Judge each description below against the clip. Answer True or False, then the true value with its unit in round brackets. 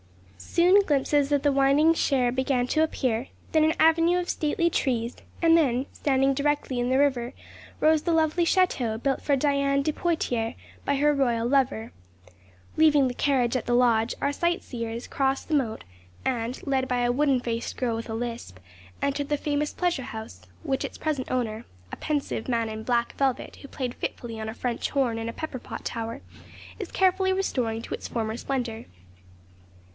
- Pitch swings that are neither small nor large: True (3.9 semitones)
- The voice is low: False (265 Hz)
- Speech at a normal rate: True (180 wpm)